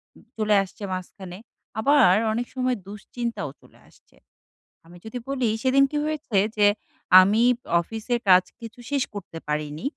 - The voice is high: Yes, high, 220 Hz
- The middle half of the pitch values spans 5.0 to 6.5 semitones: Yes, average, 5.3 semitones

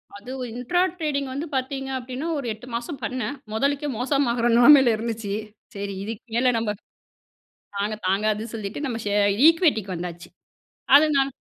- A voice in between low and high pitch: No, high, 245 Hz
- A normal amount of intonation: Yes, average, 4.4 semitones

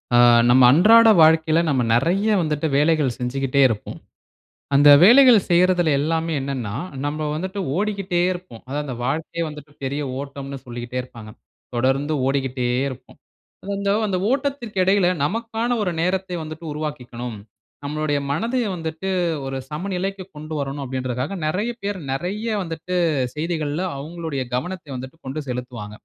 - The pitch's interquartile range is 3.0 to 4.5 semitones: No, average, 5.3 semitones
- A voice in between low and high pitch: Yes, medium, 155 Hz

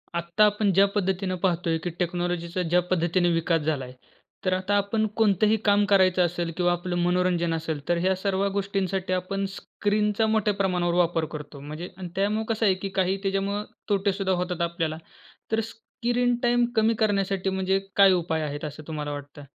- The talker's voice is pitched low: No, medium, 185 Hz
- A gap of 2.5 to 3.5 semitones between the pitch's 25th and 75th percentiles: Yes, average, 2.8 semitones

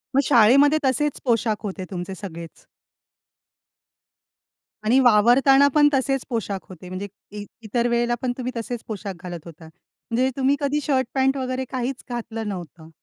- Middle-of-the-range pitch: No, high, 240 Hz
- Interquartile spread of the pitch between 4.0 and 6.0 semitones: Yes, average, 4.7 semitones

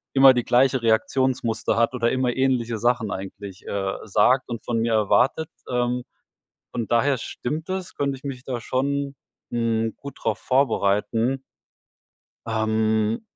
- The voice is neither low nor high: No, low, 120 Hz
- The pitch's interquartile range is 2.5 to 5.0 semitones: Yes, average, 2.9 semitones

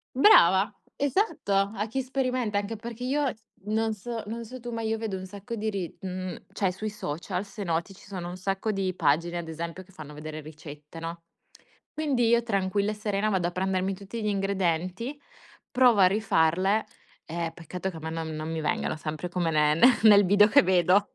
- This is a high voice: Yes, high, 195 Hz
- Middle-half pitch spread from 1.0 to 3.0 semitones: No, average, 4.2 semitones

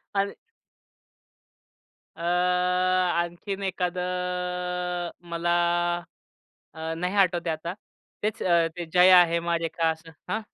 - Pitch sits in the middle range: Yes, medium, 180 Hz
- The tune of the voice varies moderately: No, narrow, 1.1 semitones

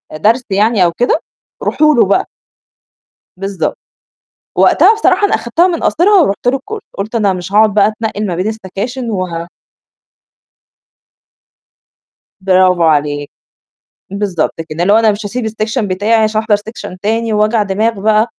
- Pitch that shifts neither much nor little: Yes, average, 3.1 semitones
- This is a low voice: No, high, 215 Hz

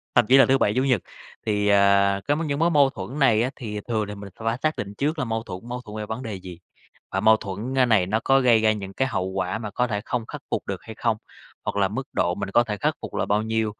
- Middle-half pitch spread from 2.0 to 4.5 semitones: Yes, average, 3.8 semitones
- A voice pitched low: Yes, low, 110 Hz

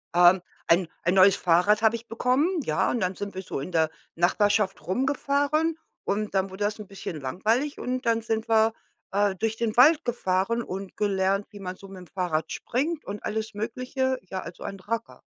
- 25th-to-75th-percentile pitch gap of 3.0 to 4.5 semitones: Yes, average, 3.8 semitones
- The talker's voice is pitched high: Yes, high, 205 Hz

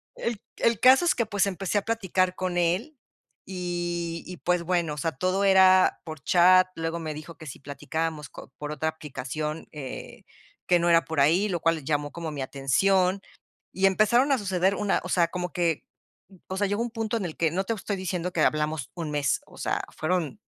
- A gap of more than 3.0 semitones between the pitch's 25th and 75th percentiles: Yes, average, 3.4 semitones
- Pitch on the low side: No, medium, 175 Hz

